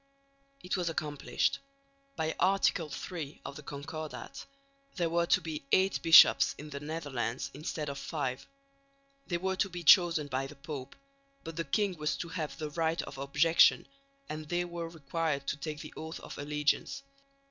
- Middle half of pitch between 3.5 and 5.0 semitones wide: No, average, 2.8 semitones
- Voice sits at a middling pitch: Yes, medium, 155 Hz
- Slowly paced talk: No, average, 170 wpm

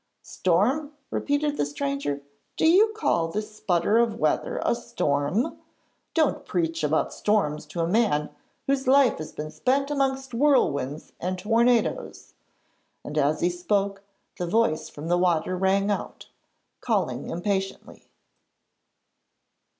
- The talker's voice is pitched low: No, high, 195 Hz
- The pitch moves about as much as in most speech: No, wide, 7.6 semitones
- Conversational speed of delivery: No, slow, 125 wpm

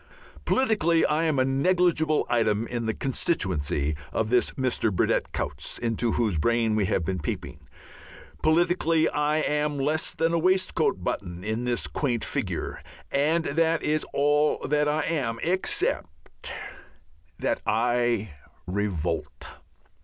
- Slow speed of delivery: Yes, slow, 130 wpm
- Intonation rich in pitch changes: Yes, wide, 6.4 semitones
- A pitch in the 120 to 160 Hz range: Yes, low, 135 Hz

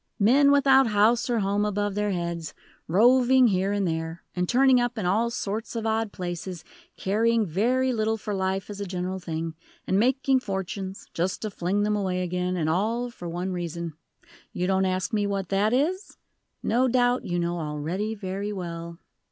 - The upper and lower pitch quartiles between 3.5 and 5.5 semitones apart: Yes, average, 4.2 semitones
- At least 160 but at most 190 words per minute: Yes, average, 180 wpm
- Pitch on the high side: Yes, high, 200 Hz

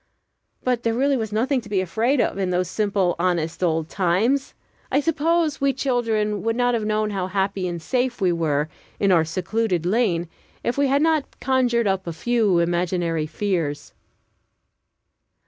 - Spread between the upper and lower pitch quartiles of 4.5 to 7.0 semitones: Yes, wide, 5.6 semitones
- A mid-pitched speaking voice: No, high, 210 Hz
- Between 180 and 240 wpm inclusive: No, average, 165 wpm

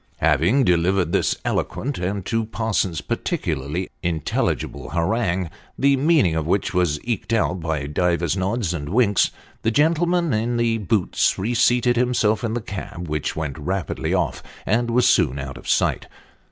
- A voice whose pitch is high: No, low, 100 Hz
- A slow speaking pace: No, average, 155 wpm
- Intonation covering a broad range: Yes, wide, 6.0 semitones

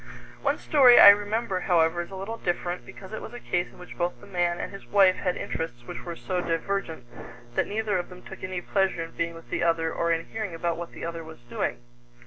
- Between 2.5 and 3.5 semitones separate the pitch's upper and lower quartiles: Yes, average, 2.9 semitones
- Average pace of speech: No, fast, 240 wpm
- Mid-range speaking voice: Yes, medium, 180 Hz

